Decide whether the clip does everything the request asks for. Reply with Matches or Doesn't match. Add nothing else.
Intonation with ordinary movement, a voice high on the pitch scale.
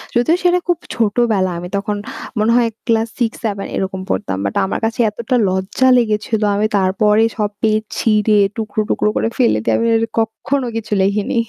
Doesn't match